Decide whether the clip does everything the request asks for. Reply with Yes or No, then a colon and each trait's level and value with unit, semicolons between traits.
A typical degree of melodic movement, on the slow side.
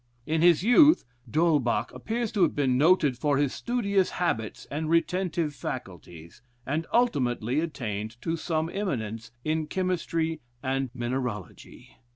No: wide, 5.9 semitones; slow, 130 wpm